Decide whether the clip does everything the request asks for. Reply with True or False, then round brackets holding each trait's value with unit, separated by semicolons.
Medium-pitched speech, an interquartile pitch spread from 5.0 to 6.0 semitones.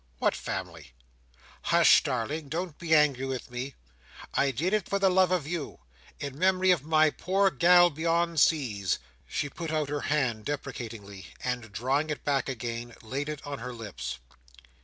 True (145 Hz; 5.4 semitones)